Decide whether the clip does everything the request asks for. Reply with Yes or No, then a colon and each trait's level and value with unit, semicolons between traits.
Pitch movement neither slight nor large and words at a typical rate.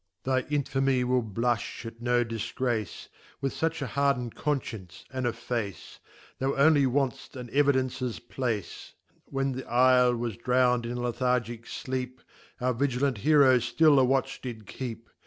No: narrow, 2.2 semitones; average, 150 wpm